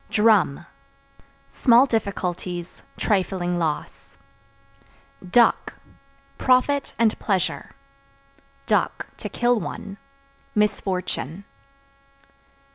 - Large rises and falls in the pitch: No, average, 4.5 semitones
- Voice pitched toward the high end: Yes, high, 200 Hz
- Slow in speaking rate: Yes, slow, 60 wpm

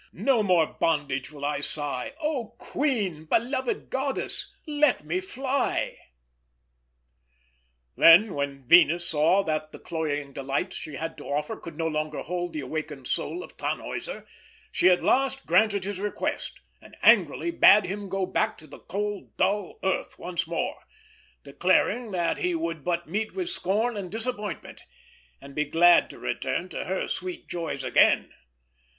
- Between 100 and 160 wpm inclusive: Yes, average, 155 wpm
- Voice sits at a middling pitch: Yes, medium, 180 Hz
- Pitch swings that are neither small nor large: No, wide, 6.1 semitones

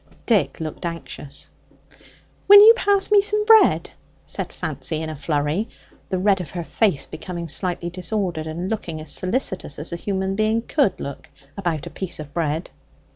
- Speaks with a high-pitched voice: No, medium, 180 Hz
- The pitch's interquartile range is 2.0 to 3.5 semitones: No, wide, 5.4 semitones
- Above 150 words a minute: Yes, average, 170 wpm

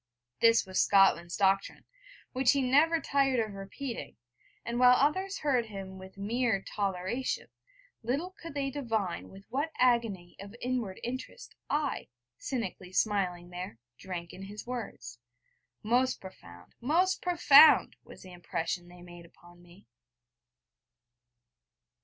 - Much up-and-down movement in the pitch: Yes, wide, 5.9 semitones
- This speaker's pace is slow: Yes, slow, 130 wpm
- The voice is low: No, high, 215 Hz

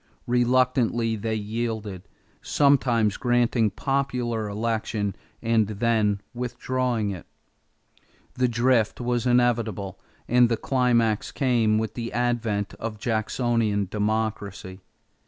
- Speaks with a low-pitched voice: Yes, low, 115 Hz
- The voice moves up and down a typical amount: No, narrow, 2.3 semitones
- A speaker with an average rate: No, slow, 100 wpm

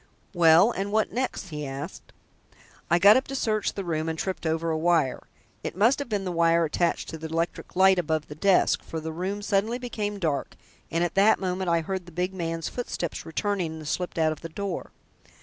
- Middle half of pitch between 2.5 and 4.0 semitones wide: Yes, average, 3.6 semitones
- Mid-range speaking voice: Yes, medium, 175 Hz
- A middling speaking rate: No, fast, 215 wpm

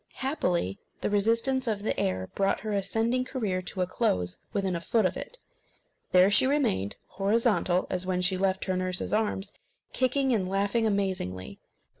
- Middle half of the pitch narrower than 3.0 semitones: No, average, 3.7 semitones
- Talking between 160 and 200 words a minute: Yes, average, 165 wpm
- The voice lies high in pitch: Yes, high, 195 Hz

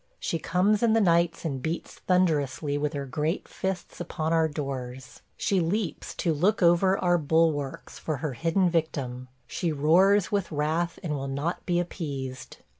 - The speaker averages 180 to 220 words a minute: No, average, 165 wpm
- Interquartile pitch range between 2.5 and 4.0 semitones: Yes, average, 3.7 semitones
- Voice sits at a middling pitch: Yes, medium, 165 Hz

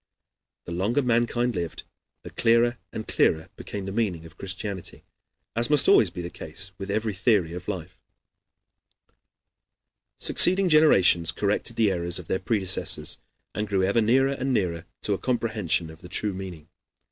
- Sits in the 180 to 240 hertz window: No, low, 100 Hz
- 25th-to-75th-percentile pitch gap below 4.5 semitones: No, average, 4.8 semitones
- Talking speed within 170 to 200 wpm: No, average, 160 wpm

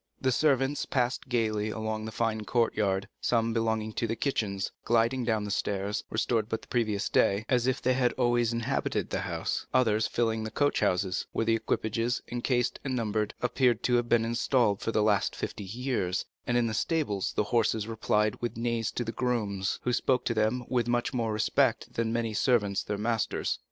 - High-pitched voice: No, low, 115 Hz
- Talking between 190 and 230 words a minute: Yes, average, 195 wpm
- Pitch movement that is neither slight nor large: No, narrow, 2.1 semitones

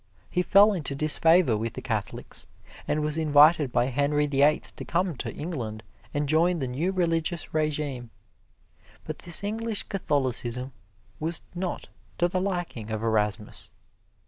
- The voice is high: No, medium, 150 Hz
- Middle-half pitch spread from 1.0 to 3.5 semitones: No, average, 5.3 semitones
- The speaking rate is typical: Yes, average, 145 wpm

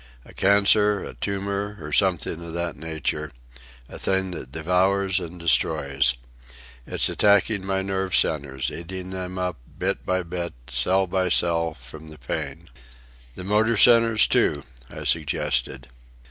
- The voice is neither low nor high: No, very low, 90 Hz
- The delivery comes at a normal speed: No, slow, 130 wpm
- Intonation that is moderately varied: Yes, average, 3.9 semitones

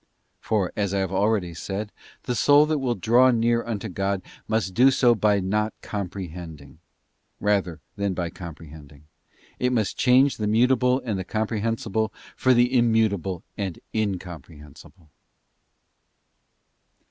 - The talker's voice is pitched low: Yes, low, 105 Hz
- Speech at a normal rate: No, slow, 130 wpm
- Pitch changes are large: No, average, 4.3 semitones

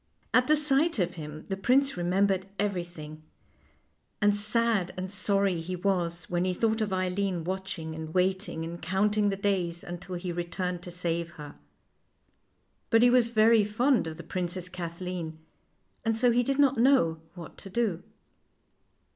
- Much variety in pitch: No, average, 3.8 semitones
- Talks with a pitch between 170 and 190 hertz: Yes, medium, 185 Hz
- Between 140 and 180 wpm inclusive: Yes, average, 165 wpm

